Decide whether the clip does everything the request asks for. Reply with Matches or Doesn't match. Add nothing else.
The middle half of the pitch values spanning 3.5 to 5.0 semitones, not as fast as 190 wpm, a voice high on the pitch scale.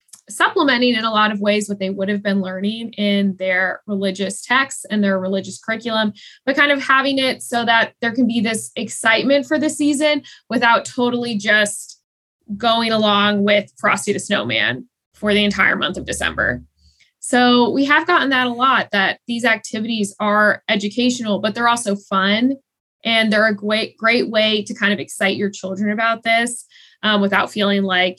Doesn't match